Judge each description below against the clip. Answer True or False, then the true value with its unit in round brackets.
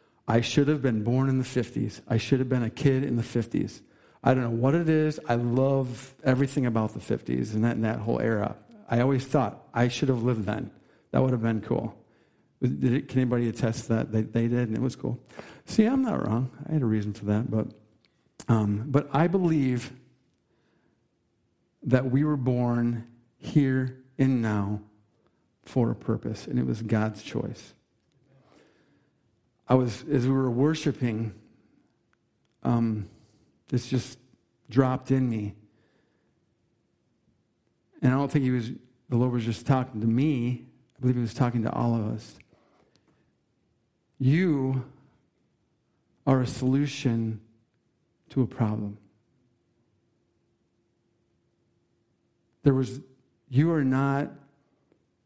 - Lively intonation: False (2.8 semitones)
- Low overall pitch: True (125 Hz)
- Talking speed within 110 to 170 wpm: True (150 wpm)